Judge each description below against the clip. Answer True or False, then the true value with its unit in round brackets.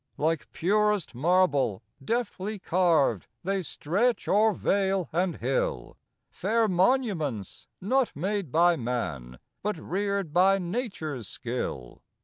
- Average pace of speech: False (110 wpm)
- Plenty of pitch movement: True (5.9 semitones)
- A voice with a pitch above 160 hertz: True (185 Hz)